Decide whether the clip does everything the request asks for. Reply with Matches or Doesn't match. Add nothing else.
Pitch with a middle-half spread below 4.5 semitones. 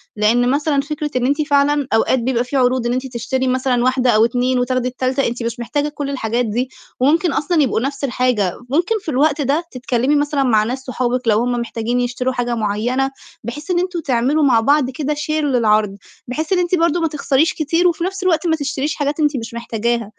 Matches